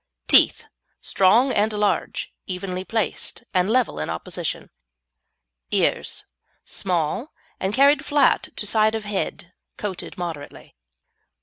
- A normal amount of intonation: Yes, average, 3.6 semitones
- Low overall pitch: No, high, 205 Hz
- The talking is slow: Yes, slow, 110 wpm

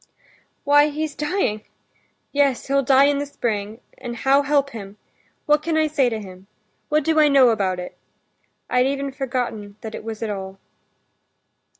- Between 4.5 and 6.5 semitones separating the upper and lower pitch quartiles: Yes, average, 4.9 semitones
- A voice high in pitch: Yes, very high, 270 Hz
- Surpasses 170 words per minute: No, average, 165 wpm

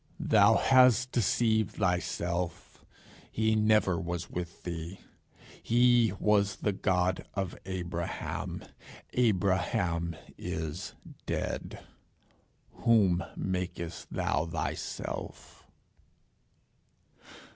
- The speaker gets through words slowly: Yes, slow, 75 wpm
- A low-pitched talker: Yes, very low, 95 Hz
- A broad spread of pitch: No, average, 4.1 semitones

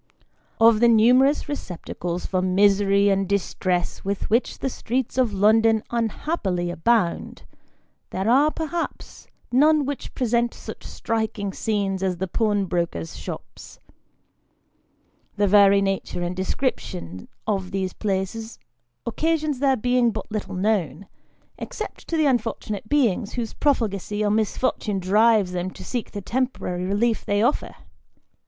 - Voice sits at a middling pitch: No, high, 210 Hz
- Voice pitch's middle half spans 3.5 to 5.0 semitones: Yes, average, 4.1 semitones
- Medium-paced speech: No, slow, 130 wpm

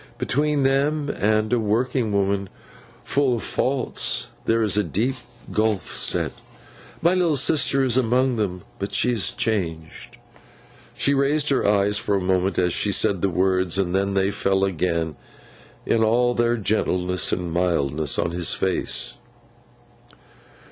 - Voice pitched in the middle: No, low, 105 Hz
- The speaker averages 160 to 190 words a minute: No, average, 150 wpm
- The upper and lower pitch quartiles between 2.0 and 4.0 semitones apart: No, average, 5.3 semitones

